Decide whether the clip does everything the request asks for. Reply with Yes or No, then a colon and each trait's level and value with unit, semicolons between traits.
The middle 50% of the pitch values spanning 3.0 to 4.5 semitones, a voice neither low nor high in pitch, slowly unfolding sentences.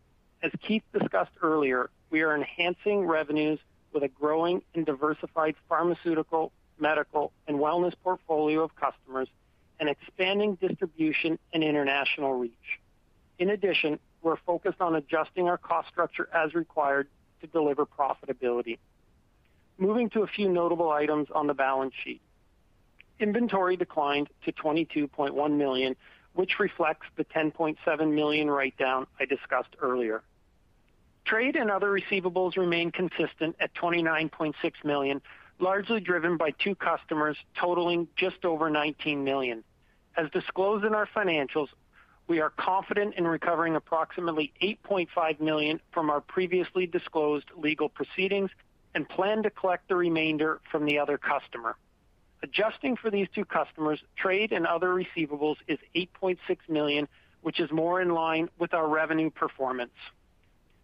Yes: average, 3.5 semitones; medium, 160 Hz; slow, 130 wpm